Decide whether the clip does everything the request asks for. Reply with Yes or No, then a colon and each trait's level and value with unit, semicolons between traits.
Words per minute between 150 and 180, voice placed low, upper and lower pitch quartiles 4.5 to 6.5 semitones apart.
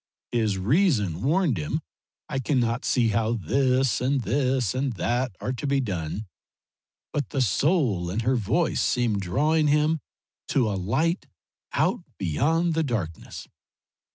No: average, 140 wpm; low, 125 Hz; wide, 5.5 semitones